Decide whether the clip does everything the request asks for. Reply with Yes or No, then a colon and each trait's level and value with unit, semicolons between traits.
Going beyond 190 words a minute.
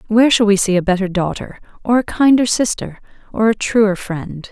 Yes: average, 200 wpm